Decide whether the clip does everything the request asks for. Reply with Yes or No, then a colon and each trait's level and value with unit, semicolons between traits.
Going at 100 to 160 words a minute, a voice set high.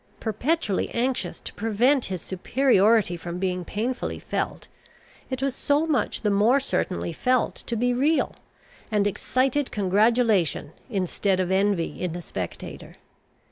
Yes: slow, 135 wpm; high, 215 Hz